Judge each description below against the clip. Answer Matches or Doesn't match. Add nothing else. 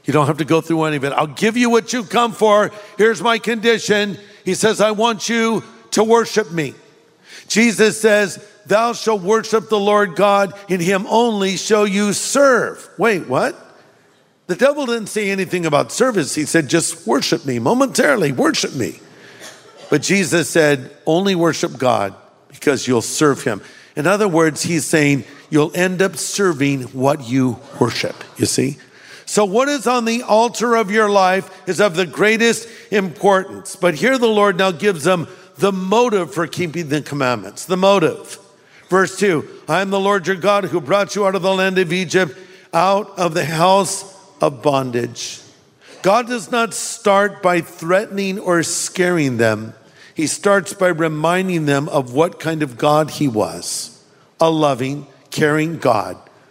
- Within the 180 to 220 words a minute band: Doesn't match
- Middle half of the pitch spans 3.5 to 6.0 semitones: Matches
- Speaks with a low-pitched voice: Doesn't match